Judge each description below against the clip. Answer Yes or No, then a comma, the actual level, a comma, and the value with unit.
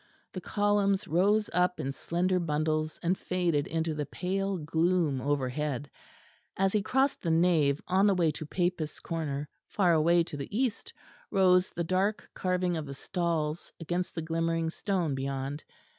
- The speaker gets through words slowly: No, average, 160 wpm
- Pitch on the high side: No, medium, 170 Hz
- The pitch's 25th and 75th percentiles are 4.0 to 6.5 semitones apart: No, average, 3.3 semitones